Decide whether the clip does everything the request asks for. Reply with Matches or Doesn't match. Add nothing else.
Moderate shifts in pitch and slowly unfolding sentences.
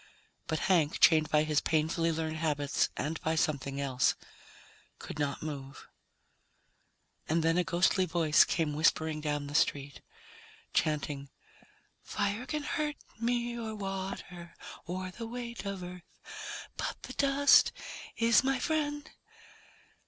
Doesn't match